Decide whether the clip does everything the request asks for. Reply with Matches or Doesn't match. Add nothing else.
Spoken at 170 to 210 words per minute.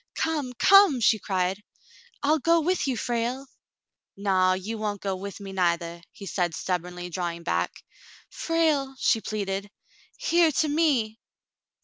Doesn't match